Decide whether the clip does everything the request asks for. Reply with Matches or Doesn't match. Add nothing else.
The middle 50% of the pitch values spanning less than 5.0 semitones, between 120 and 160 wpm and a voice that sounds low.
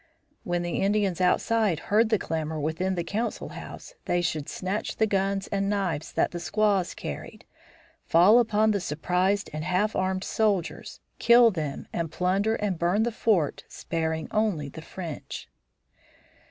Doesn't match